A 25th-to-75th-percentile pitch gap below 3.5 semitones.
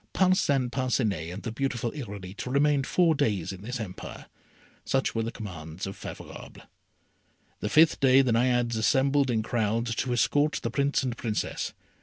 No: average, 3.9 semitones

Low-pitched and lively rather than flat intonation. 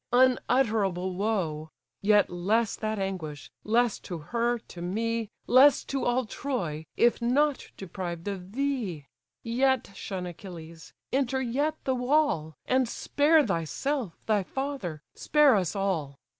No: high, 220 Hz; wide, 6.5 semitones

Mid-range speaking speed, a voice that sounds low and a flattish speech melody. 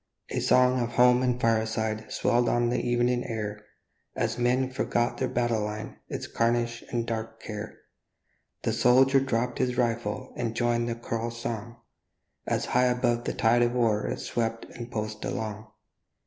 Yes: average, 160 wpm; low, 120 Hz; narrow, 1.5 semitones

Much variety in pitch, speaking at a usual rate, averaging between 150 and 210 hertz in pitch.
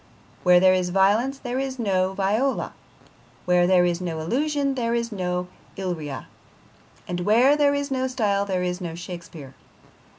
Yes: wide, 6.1 semitones; average, 160 wpm; high, 190 Hz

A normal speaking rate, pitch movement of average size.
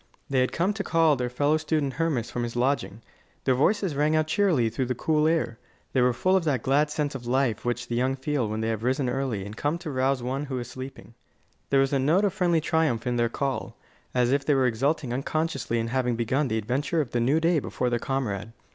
No: fast, 245 wpm; average, 4.0 semitones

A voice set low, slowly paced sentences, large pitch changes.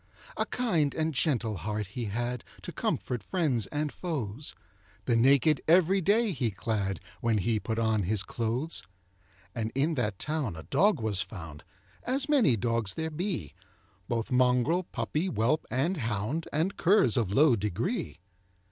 No: low, 125 Hz; average, 155 wpm; wide, 6.5 semitones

